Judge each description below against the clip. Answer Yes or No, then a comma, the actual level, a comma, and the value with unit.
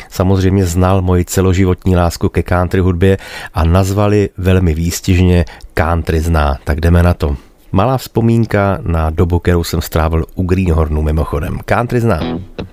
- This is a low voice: Yes, very low, 90 Hz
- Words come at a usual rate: Yes, average, 140 wpm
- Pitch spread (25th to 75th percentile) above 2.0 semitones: Yes, narrow, 2.5 semitones